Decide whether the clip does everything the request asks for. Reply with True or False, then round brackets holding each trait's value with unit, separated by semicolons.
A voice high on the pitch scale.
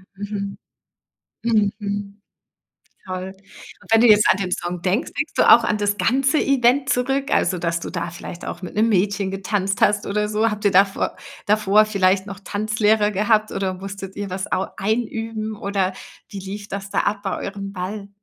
True (205 Hz)